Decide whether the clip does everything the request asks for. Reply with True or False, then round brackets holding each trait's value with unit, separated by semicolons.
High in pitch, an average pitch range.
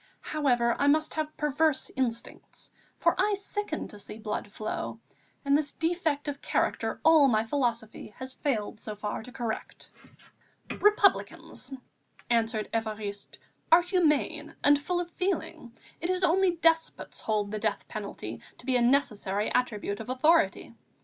False (275 Hz; 6.4 semitones)